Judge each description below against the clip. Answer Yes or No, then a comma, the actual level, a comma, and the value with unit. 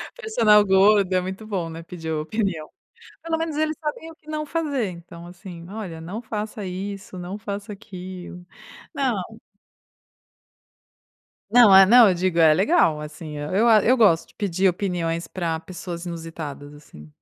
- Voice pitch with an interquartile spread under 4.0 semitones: No, average, 4.5 semitones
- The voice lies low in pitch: No, high, 190 Hz